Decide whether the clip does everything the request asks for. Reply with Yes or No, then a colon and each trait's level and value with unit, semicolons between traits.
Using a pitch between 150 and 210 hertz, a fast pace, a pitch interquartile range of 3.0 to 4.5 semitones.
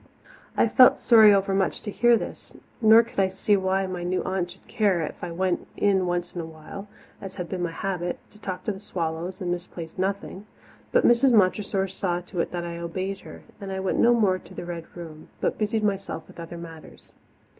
No: high, 190 Hz; fast, 215 wpm; narrow, 2.5 semitones